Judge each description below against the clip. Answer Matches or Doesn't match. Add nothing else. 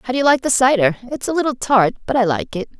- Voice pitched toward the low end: Doesn't match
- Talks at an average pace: Doesn't match